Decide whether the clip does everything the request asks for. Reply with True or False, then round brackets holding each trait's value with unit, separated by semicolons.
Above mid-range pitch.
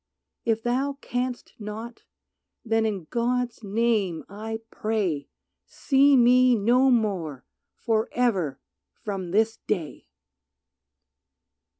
True (225 Hz)